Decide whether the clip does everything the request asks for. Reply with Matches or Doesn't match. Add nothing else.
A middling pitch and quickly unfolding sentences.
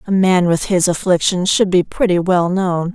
Doesn't match